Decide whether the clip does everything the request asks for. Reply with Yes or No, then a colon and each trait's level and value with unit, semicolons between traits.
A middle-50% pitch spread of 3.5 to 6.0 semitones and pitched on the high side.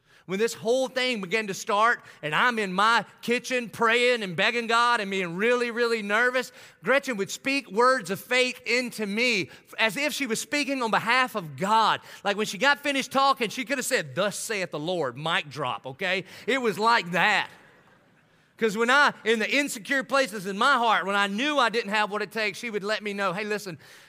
Yes: average, 3.8 semitones; high, 225 Hz